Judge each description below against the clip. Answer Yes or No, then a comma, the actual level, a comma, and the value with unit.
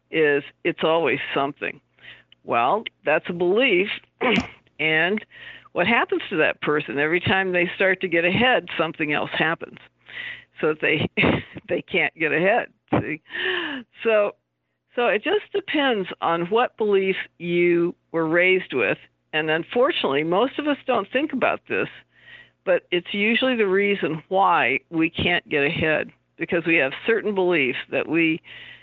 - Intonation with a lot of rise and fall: Yes, wide, 7.0 semitones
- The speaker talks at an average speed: Yes, average, 145 wpm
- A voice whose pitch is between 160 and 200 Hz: Yes, medium, 185 Hz